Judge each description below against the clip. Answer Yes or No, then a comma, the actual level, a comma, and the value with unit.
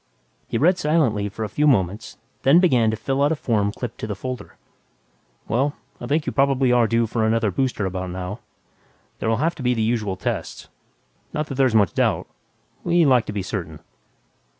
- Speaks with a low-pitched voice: Yes, low, 115 Hz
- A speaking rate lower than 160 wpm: No, average, 195 wpm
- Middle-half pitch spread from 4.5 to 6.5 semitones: Yes, average, 4.8 semitones